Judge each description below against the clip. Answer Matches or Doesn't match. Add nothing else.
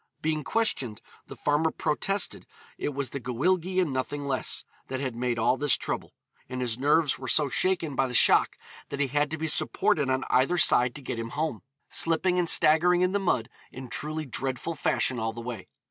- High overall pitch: Doesn't match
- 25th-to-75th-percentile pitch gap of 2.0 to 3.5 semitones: Doesn't match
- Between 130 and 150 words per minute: Doesn't match